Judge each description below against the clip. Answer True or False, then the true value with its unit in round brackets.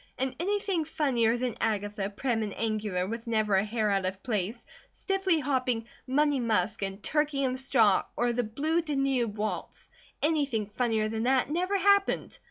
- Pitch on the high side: True (240 Hz)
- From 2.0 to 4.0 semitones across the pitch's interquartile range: False (5.3 semitones)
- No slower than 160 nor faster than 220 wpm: True (170 wpm)